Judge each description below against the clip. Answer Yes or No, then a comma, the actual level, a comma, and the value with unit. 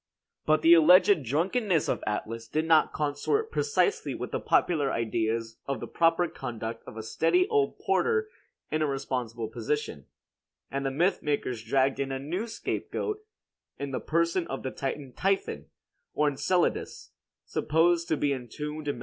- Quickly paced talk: No, average, 160 wpm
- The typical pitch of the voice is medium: Yes, medium, 150 Hz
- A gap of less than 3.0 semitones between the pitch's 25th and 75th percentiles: No, average, 5.2 semitones